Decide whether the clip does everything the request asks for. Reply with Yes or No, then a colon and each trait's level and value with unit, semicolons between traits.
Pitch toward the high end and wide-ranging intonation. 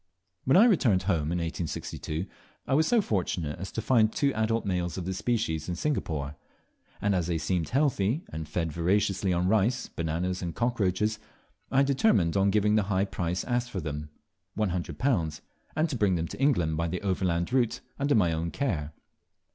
No: very low, 95 Hz; wide, 5.7 semitones